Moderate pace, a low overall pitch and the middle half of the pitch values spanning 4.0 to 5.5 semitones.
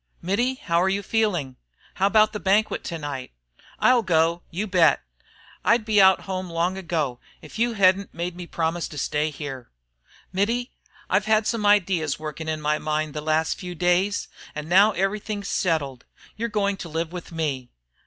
No: average, 175 wpm; medium, 180 Hz; average, 4.5 semitones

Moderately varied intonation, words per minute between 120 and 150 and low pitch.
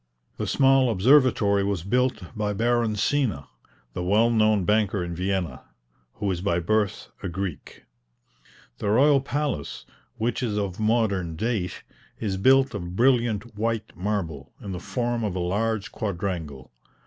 Yes: average, 4.1 semitones; average, 145 wpm; low, 105 Hz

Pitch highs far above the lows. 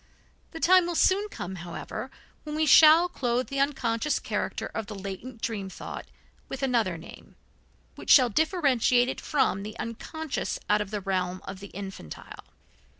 Yes: wide, 7.4 semitones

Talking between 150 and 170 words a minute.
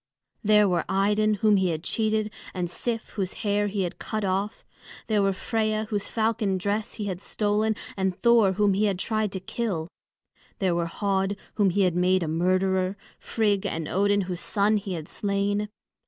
No: average, 185 wpm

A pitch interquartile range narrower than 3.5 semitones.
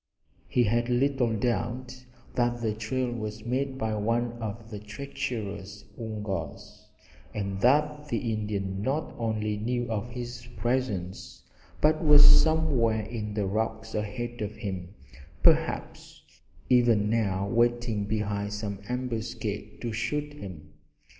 Yes: average, 2.8 semitones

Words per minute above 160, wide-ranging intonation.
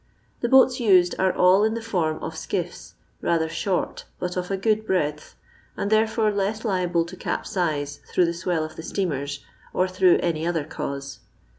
No: average, 175 wpm; average, 3.9 semitones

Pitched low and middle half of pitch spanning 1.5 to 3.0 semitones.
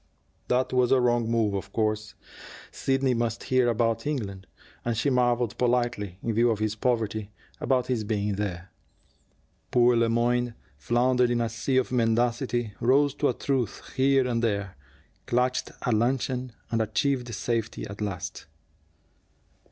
Yes: low, 120 Hz; narrow, 2.5 semitones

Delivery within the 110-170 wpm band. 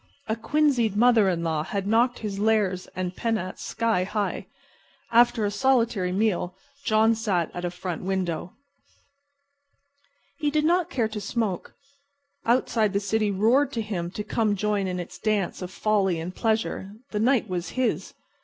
Yes: average, 160 wpm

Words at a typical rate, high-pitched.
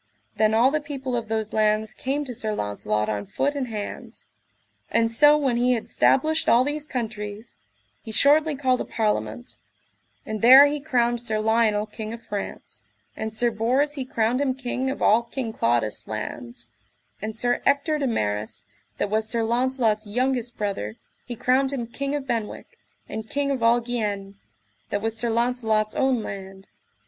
Yes: average, 175 wpm; high, 235 Hz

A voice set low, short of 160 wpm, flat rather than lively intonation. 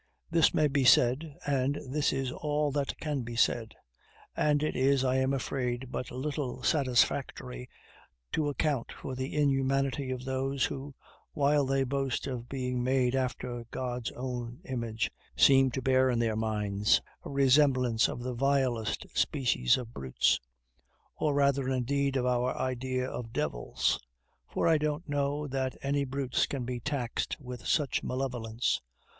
Yes: low, 130 Hz; average, 150 wpm; narrow, 2.2 semitones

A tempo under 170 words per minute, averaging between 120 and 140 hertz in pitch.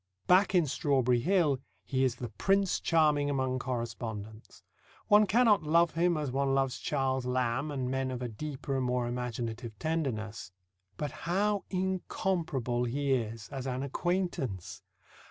Yes: average, 145 wpm; low, 135 Hz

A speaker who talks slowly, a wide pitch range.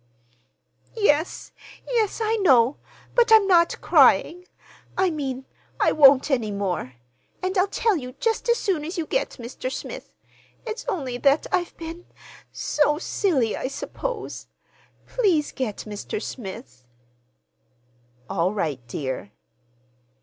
Yes: slow, 120 wpm; wide, 8.3 semitones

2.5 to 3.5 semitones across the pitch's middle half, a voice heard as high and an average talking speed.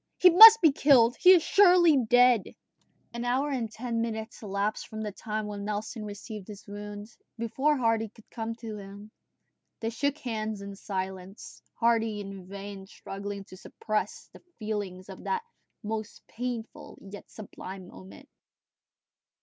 Yes: average, 3.0 semitones; high, 215 Hz; average, 150 wpm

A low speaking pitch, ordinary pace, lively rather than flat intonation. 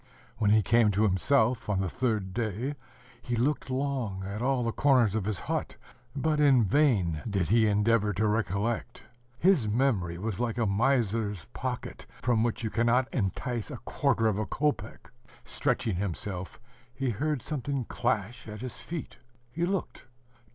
No: low, 115 Hz; average, 160 wpm; average, 3.9 semitones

